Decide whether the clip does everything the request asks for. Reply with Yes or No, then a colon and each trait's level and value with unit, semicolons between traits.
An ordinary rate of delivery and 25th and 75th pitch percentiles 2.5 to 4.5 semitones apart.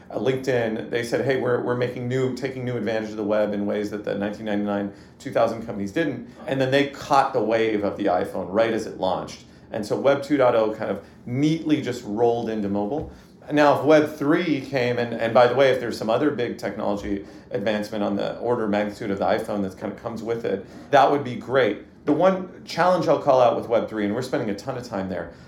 No: fast, 230 wpm; average, 4.1 semitones